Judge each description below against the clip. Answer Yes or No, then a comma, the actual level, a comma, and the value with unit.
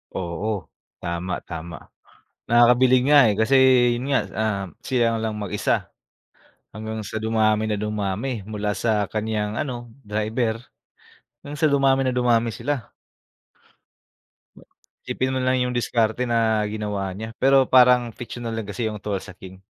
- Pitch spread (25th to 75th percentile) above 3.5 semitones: No, average, 2.9 semitones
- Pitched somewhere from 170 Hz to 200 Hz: No, low, 110 Hz